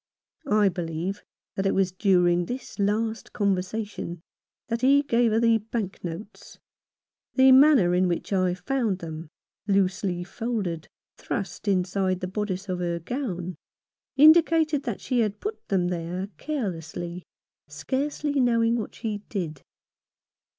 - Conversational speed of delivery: No, slow, 130 wpm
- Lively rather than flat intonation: No, average, 4.7 semitones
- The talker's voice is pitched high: Yes, high, 200 Hz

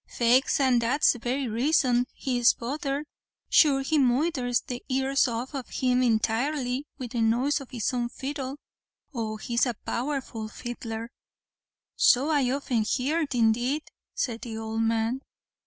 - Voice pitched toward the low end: No, very high, 250 Hz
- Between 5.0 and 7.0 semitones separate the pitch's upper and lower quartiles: No, average, 2.7 semitones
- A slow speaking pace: No, average, 150 wpm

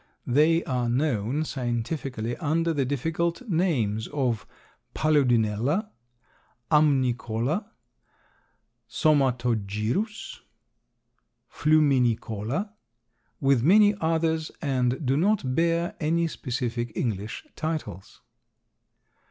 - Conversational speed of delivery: No, slow, 75 wpm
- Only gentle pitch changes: No, wide, 5.4 semitones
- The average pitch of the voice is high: No, medium, 140 Hz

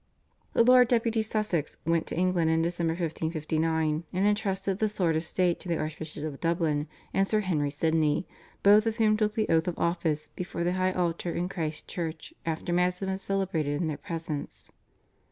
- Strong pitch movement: No, average, 3.3 semitones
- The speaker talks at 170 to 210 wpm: Yes, average, 190 wpm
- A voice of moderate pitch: Yes, medium, 170 Hz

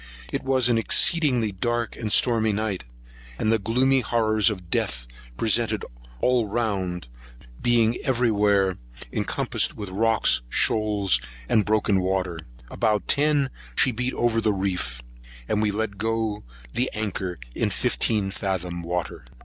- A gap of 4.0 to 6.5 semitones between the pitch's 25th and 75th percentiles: No, average, 3.4 semitones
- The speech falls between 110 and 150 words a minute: Yes, slow, 135 wpm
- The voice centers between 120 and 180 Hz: No, low, 110 Hz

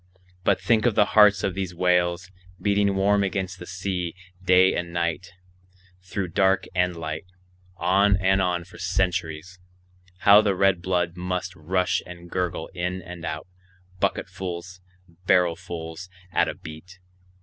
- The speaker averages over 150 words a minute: No, average, 140 wpm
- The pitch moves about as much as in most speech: No, narrow, 1.6 semitones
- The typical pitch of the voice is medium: No, very low, 90 Hz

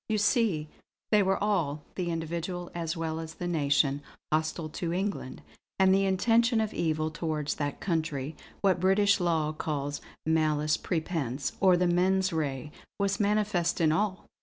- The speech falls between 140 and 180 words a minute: Yes, average, 155 wpm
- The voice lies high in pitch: No, medium, 170 Hz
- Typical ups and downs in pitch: Yes, average, 3.7 semitones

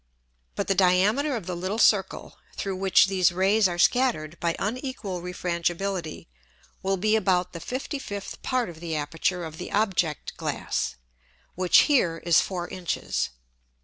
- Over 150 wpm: No, average, 145 wpm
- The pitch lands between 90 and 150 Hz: No, medium, 185 Hz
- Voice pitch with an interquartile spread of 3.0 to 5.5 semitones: Yes, average, 3.3 semitones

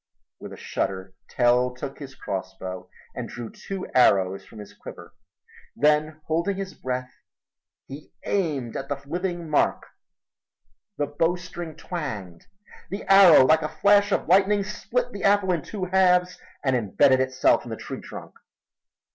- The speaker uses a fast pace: No, average, 145 wpm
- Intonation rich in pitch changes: Yes, wide, 6.6 semitones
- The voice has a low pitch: No, medium, 150 Hz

